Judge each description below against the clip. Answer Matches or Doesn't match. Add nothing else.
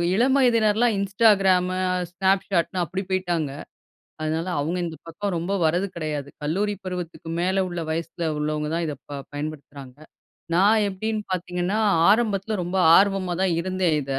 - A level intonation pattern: Doesn't match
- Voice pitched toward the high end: Doesn't match